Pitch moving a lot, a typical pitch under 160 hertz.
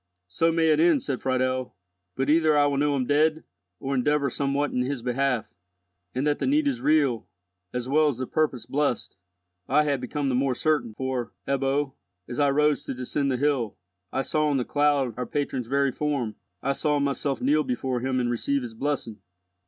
No: narrow, 2.6 semitones; medium, 140 Hz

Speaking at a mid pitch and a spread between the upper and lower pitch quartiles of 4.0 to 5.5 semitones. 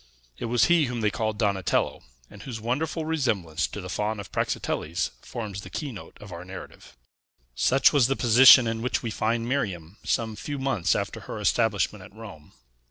No: low, 110 Hz; average, 4.4 semitones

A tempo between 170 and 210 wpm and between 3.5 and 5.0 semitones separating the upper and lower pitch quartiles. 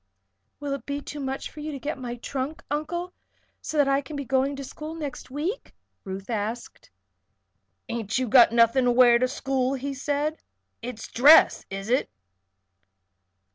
No: average, 175 wpm; average, 3.1 semitones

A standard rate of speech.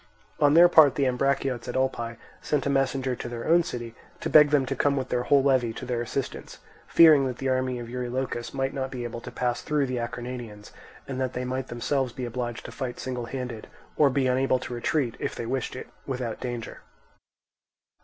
No: fast, 210 wpm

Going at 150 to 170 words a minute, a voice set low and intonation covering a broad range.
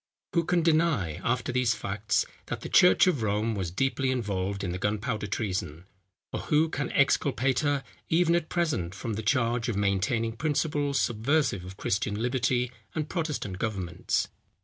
Yes: average, 160 wpm; low, 120 Hz; wide, 6.2 semitones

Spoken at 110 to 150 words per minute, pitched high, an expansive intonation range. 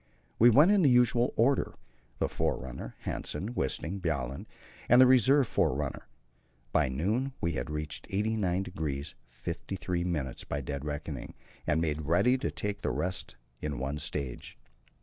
No: average, 140 wpm; very low, 85 Hz; wide, 7.7 semitones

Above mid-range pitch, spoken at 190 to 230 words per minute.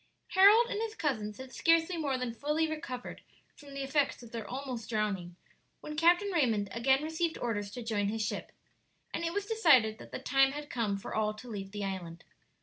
Yes: very high, 260 Hz; average, 200 wpm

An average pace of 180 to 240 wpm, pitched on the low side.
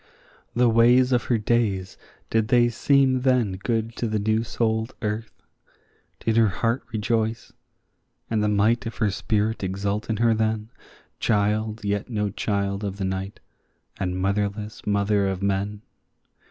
No: average, 150 wpm; low, 110 Hz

